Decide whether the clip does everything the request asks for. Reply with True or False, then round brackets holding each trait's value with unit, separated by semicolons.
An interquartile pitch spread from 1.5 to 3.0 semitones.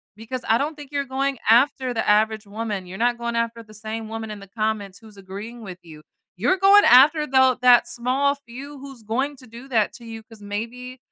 False (3.4 semitones)